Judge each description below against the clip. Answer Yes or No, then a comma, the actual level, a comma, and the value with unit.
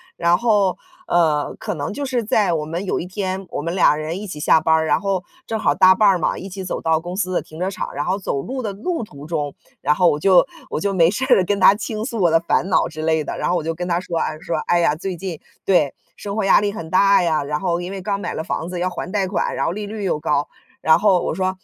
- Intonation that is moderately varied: Yes, average, 3.5 semitones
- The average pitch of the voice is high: No, medium, 180 Hz